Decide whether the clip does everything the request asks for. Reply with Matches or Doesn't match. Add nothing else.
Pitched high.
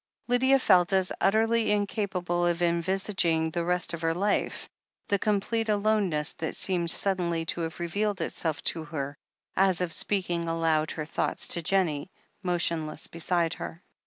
Doesn't match